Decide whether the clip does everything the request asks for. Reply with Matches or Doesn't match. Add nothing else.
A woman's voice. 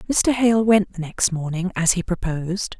Matches